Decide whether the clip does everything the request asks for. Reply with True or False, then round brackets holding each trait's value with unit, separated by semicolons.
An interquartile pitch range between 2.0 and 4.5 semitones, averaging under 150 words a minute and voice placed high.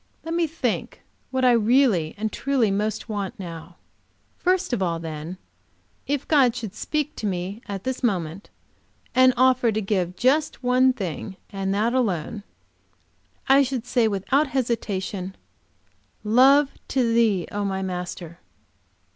False (5.3 semitones; 140 wpm; 220 Hz)